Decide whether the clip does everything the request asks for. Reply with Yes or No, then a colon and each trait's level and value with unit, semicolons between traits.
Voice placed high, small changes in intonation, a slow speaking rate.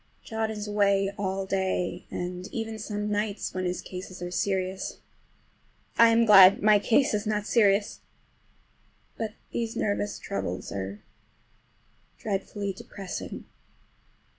Yes: high, 200 Hz; narrow, 2.3 semitones; slow, 120 wpm